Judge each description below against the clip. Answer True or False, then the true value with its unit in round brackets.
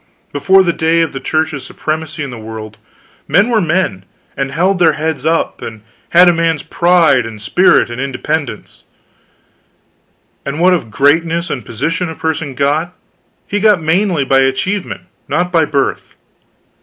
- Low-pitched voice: False (160 Hz)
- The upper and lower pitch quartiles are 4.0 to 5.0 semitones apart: True (4.3 semitones)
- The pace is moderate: True (155 wpm)